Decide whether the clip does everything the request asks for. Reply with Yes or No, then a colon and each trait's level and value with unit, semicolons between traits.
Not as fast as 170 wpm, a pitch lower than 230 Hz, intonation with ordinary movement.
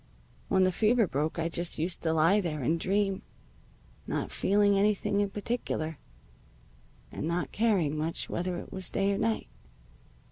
Yes: average, 155 wpm; medium, 185 Hz; average, 3.8 semitones